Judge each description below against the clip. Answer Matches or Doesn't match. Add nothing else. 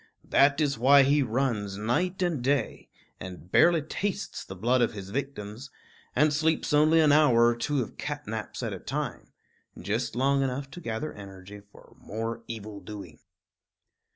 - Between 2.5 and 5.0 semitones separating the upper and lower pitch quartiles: Doesn't match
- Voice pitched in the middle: Doesn't match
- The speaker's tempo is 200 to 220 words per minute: Doesn't match